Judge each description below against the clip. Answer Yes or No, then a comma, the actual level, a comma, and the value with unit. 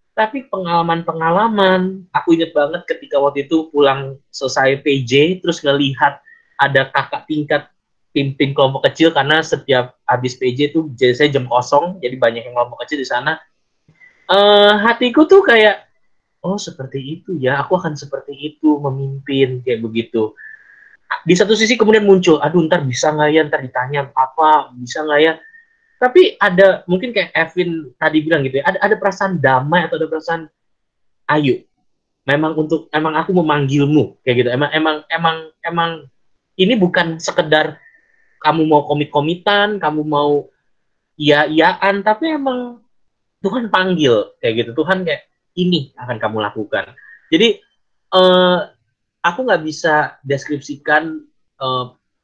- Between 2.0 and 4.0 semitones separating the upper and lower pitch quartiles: No, average, 5.1 semitones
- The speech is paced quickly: Yes, fast, 145 wpm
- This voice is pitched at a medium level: Yes, medium, 155 Hz